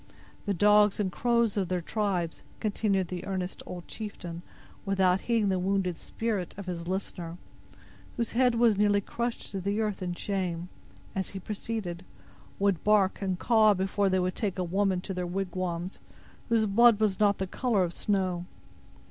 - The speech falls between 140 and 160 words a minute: No, average, 175 wpm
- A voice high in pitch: Yes, high, 195 Hz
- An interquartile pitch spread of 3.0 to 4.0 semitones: No, narrow, 2.5 semitones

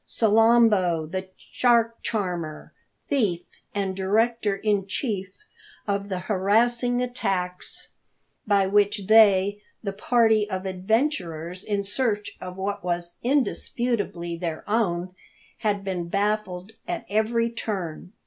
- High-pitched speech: Yes, high, 200 Hz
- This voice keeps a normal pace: No, slow, 110 wpm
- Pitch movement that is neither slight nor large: Yes, average, 3.4 semitones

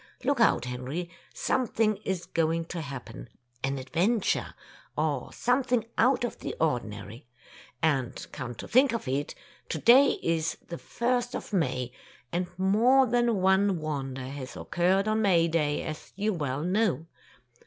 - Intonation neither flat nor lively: No, wide, 8.0 semitones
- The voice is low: No, medium, 170 Hz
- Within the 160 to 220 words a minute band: No, average, 150 wpm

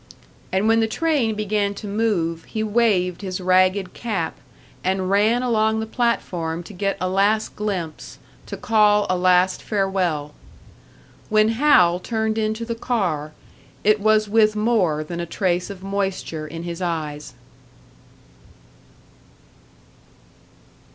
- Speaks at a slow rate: Yes, slow, 130 wpm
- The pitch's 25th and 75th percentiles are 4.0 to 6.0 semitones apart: No, average, 3.4 semitones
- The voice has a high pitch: Yes, high, 200 Hz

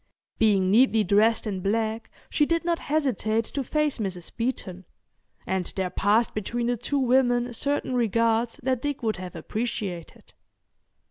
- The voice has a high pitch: Yes, high, 230 Hz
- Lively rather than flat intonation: No, average, 4.0 semitones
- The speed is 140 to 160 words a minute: Yes, average, 145 wpm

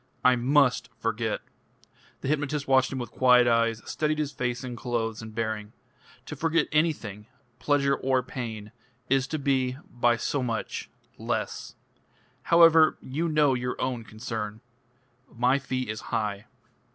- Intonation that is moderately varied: Yes, average, 3.4 semitones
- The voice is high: No, low, 125 Hz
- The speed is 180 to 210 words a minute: No, average, 140 wpm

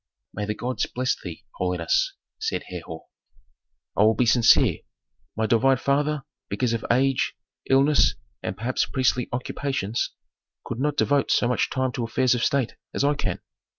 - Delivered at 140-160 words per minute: Yes, average, 155 wpm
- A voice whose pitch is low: Yes, low, 125 Hz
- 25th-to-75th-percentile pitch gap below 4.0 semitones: Yes, average, 3.3 semitones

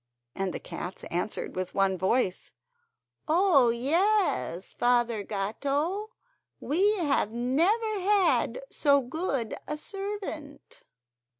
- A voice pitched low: No, very high, 280 Hz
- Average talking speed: No, slow, 100 wpm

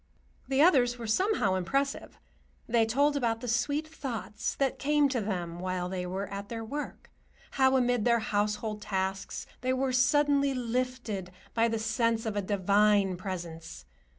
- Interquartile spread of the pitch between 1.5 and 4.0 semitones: No, average, 4.8 semitones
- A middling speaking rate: Yes, average, 155 wpm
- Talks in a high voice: Yes, high, 225 Hz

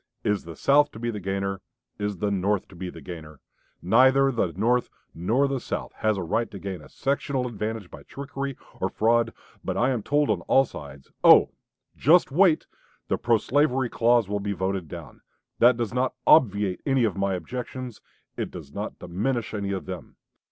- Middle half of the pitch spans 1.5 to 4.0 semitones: No, average, 5.0 semitones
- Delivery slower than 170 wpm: No, average, 190 wpm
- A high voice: No, low, 110 Hz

